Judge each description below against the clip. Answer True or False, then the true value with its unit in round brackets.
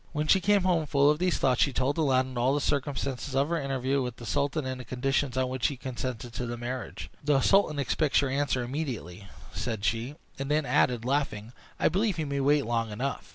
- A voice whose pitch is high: False (135 Hz)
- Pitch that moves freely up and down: False (2.9 semitones)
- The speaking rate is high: True (220 wpm)